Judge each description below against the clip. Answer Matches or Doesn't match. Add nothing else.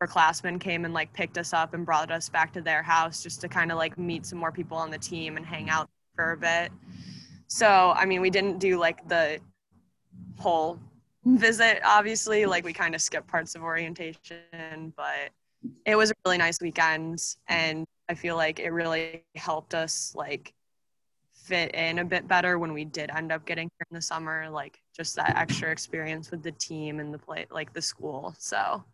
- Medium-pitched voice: Matches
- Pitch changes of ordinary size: Doesn't match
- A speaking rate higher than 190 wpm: Matches